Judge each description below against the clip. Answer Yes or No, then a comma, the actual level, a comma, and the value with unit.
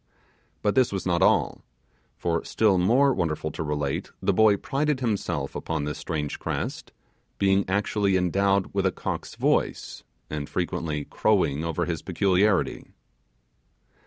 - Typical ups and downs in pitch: Yes, average, 4.2 semitones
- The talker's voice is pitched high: No, very low, 95 Hz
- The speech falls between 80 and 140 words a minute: Yes, slow, 135 wpm